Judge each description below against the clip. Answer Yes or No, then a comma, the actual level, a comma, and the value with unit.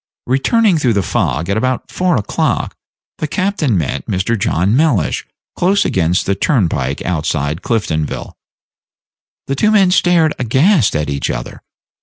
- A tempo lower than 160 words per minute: Yes, average, 140 wpm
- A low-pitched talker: Yes, low, 115 Hz